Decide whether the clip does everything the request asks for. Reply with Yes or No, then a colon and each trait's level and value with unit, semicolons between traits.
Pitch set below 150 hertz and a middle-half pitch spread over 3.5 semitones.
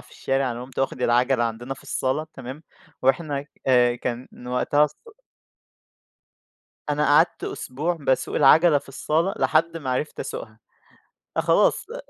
No: low, 135 Hz; average, 3.2 semitones